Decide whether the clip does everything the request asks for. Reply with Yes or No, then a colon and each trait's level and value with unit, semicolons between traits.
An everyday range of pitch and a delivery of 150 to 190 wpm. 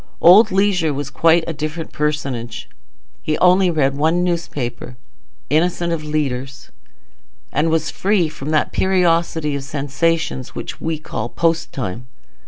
No: average, 3.3 semitones; slow, 135 wpm